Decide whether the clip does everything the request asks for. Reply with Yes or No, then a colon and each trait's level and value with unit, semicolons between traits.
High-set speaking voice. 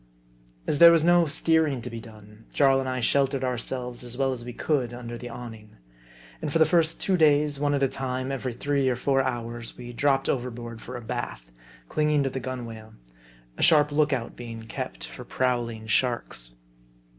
No: low, 130 Hz